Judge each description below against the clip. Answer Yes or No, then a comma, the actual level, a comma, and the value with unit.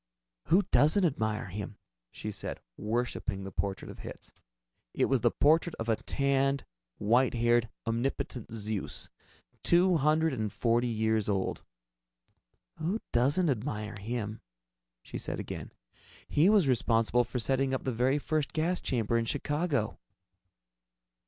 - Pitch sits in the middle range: No, low, 120 Hz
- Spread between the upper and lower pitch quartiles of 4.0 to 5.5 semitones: Yes, average, 4.8 semitones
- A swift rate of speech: No, slow, 135 wpm